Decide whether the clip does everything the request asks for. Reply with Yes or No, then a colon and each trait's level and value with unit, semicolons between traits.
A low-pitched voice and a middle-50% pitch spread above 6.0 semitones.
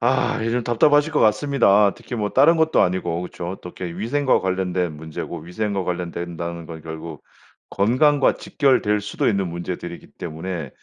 No: very low, 95 Hz; wide, 5.6 semitones